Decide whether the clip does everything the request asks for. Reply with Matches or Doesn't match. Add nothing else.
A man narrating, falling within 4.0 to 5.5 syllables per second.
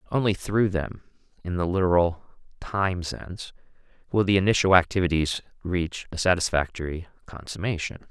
Matches